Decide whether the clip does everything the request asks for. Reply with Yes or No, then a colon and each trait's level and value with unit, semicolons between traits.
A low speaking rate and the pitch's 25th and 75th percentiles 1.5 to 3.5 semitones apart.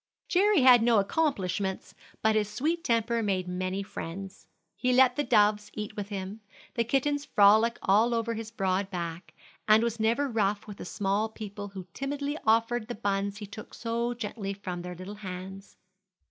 No: average, 175 wpm; average, 3.1 semitones